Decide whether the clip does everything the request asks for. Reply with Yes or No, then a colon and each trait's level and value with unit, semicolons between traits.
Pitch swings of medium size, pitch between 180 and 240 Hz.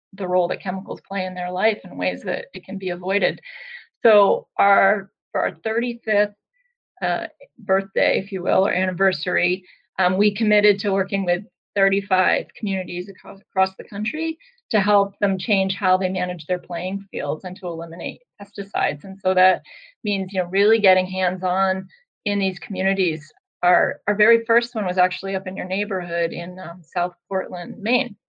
No: narrow, 2.2 semitones; high, 190 Hz